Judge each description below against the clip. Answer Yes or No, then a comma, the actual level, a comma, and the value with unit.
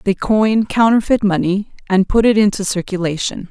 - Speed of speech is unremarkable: Yes, average, 155 wpm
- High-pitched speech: Yes, high, 205 Hz